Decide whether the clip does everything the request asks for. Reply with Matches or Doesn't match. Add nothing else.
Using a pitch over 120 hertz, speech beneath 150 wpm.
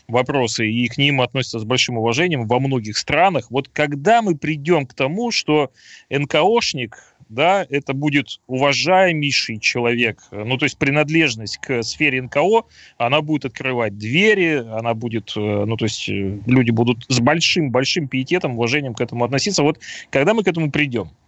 Doesn't match